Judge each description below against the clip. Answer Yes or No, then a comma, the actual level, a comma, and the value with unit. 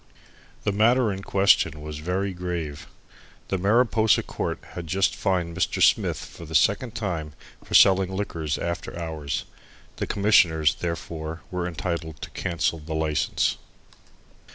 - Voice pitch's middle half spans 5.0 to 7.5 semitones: No, average, 3.6 semitones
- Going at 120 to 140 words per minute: Yes, slow, 135 wpm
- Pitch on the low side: Yes, very low, 85 Hz